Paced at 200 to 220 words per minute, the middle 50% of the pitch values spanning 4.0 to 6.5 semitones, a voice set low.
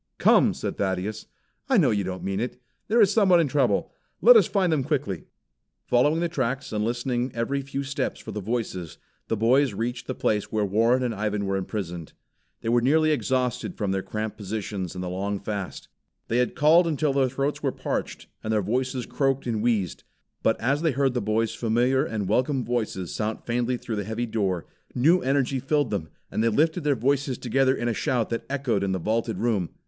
Yes: fast, 205 wpm; average, 4.5 semitones; low, 120 Hz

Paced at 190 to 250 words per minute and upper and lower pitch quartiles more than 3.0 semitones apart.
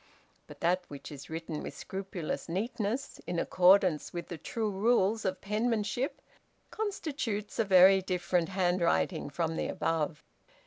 No: slow, 135 wpm; average, 3.7 semitones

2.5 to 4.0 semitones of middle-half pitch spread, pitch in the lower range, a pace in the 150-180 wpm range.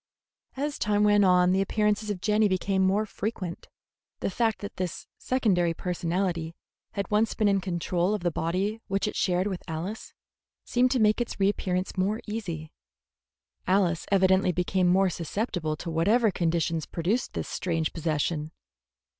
No: average, 3.4 semitones; high, 190 Hz; average, 155 wpm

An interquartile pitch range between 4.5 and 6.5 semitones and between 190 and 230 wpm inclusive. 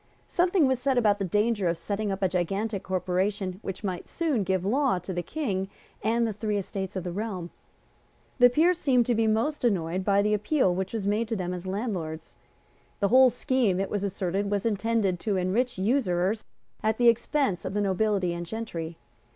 No: average, 3.7 semitones; average, 200 wpm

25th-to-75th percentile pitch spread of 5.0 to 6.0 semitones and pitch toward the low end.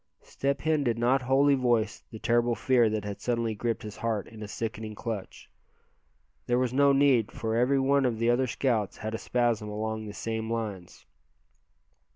No: average, 2.7 semitones; low, 115 Hz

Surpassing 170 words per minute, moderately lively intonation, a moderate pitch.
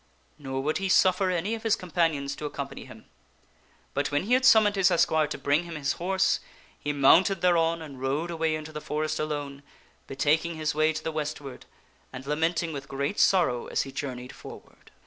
Yes: average, 200 wpm; average, 3.6 semitones; medium, 155 Hz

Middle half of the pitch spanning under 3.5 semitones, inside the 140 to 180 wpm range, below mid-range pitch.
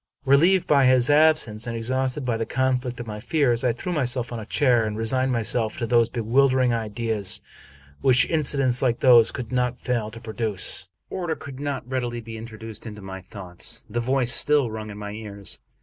No: average, 2.8 semitones; average, 195 wpm; low, 120 Hz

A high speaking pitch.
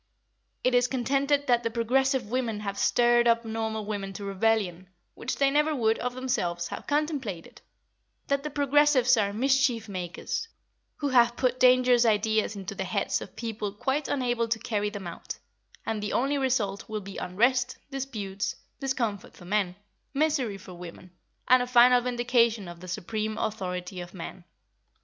Yes: high, 230 Hz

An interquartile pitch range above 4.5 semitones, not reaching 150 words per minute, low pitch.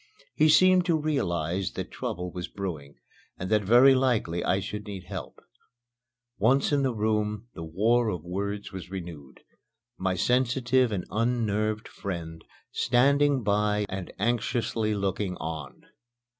Yes: average, 5.0 semitones; slow, 135 wpm; low, 105 Hz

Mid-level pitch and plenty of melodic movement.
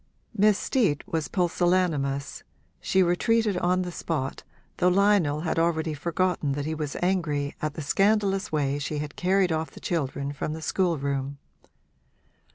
No: medium, 165 Hz; average, 4.2 semitones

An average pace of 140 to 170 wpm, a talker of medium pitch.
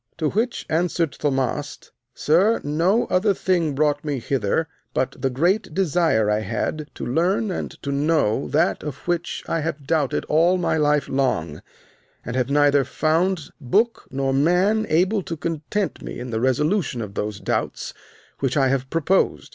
Yes: average, 165 wpm; medium, 150 Hz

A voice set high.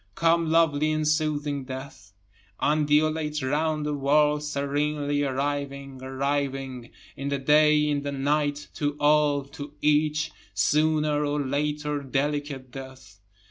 No: medium, 145 Hz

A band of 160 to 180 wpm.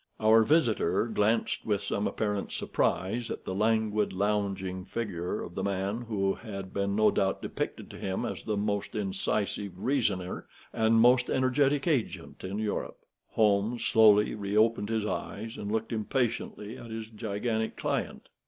No: average, 150 wpm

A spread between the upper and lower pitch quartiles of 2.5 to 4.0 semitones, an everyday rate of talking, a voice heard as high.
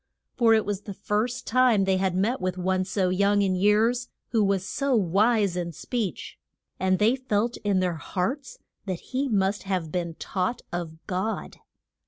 Yes: average, 3.4 semitones; average, 175 wpm; high, 200 Hz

